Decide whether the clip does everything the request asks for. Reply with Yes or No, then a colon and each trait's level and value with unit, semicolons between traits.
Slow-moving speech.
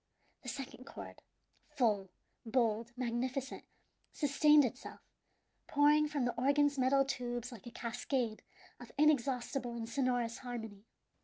Yes: slow, 115 wpm